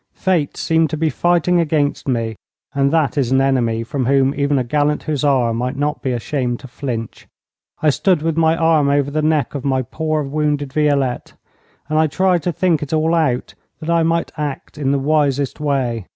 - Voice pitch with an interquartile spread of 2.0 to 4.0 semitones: Yes, average, 2.8 semitones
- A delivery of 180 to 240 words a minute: Yes, average, 195 wpm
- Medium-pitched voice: Yes, medium, 145 Hz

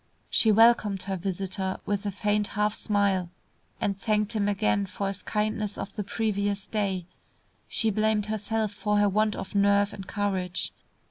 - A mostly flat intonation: Yes, narrow, 1.4 semitones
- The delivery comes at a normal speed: Yes, average, 160 wpm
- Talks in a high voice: Yes, high, 205 Hz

